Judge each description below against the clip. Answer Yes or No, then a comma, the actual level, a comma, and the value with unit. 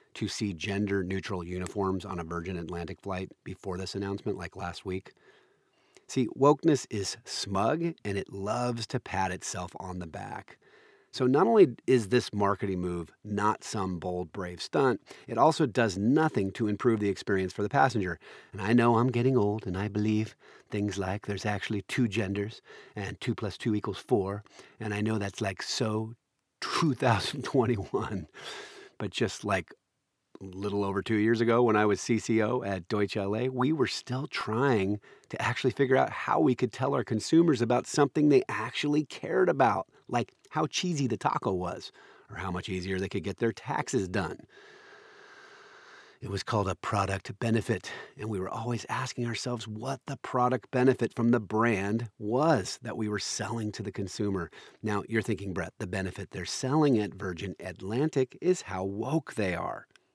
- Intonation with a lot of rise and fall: No, average, 4.1 semitones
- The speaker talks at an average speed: Yes, average, 175 wpm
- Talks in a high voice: No, low, 110 Hz